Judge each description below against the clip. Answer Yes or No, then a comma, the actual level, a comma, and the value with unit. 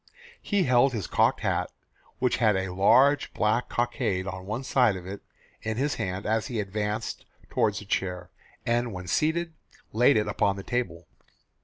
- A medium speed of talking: Yes, average, 170 wpm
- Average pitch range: Yes, average, 4.3 semitones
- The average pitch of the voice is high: No, low, 110 Hz